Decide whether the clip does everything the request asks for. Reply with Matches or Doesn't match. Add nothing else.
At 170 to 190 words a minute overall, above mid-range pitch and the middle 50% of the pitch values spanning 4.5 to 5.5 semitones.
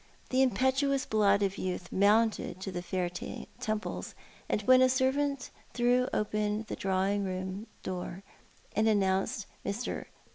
Doesn't match